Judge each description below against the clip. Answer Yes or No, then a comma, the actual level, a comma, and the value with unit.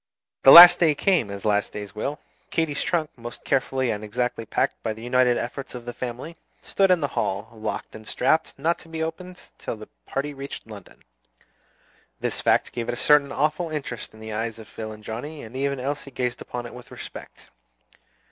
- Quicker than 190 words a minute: Yes, fast, 205 wpm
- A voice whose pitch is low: Yes, low, 125 Hz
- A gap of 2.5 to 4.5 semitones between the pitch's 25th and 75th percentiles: No, average, 5.0 semitones